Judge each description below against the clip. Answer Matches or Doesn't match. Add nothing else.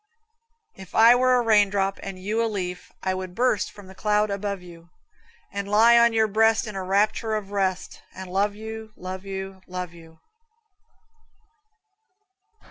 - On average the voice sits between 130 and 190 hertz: Doesn't match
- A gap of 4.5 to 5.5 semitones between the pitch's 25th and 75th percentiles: Doesn't match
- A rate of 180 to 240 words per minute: Doesn't match